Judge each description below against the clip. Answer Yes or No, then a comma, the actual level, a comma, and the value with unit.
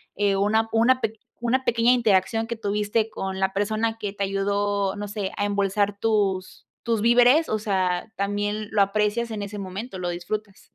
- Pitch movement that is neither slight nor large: No, narrow, 2.2 semitones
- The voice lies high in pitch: Yes, high, 205 Hz